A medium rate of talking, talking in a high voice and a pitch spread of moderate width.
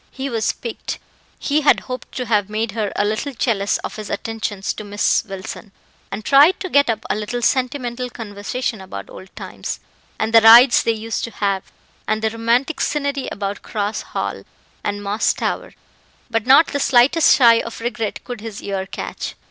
Yes: average, 180 wpm; high, 225 Hz; average, 3.4 semitones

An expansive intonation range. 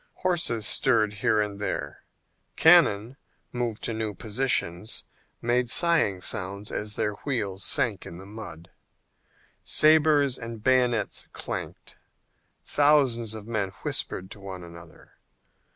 No: average, 4.3 semitones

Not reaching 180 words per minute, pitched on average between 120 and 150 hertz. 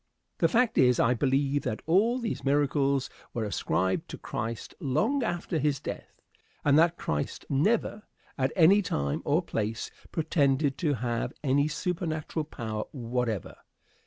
Yes: average, 140 wpm; medium, 140 Hz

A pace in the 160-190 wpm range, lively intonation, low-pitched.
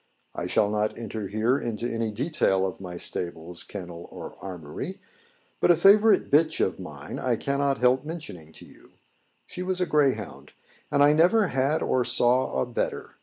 Yes: average, 170 wpm; wide, 7.7 semitones; low, 125 Hz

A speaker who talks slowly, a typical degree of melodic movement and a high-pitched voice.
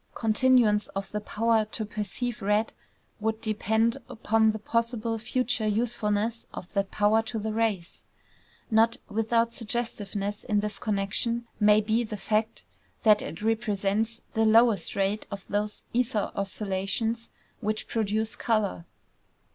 No: slow, 130 wpm; narrow, 1.6 semitones; high, 215 Hz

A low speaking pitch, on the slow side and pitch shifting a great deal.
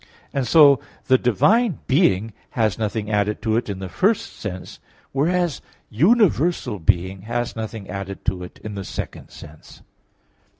No: low, 110 Hz; average, 145 wpm; wide, 6.4 semitones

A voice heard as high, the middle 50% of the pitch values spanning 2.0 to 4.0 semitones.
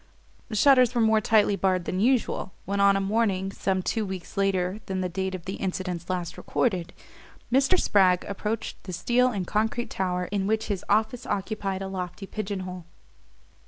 Yes: high, 195 Hz; average, 2.8 semitones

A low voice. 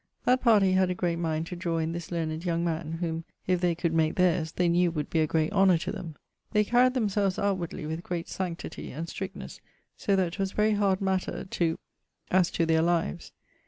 No: medium, 175 Hz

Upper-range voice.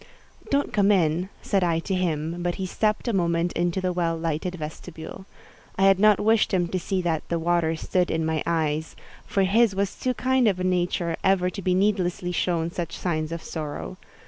No: medium, 180 Hz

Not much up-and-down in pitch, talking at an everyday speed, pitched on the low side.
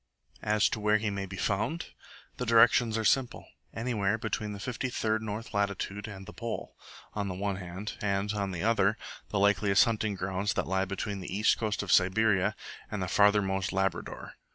Yes: narrow, 2.1 semitones; average, 175 wpm; low, 105 Hz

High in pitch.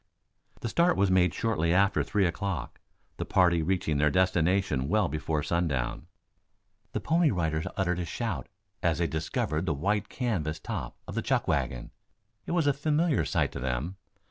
No: very low, 90 Hz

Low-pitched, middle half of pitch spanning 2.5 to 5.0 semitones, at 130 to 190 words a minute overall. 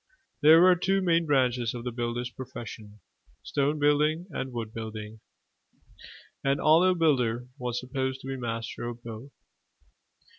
Yes: low, 130 Hz; average, 4.1 semitones; average, 140 wpm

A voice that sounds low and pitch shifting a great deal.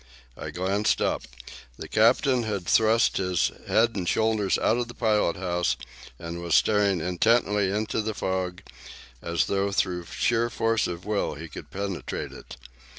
No: low, 100 Hz; average, 3.7 semitones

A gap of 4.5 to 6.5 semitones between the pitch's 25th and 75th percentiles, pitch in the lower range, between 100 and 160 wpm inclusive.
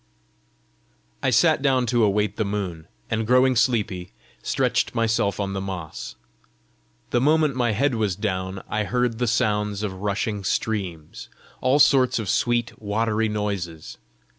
No: average, 3.6 semitones; low, 110 Hz; average, 140 wpm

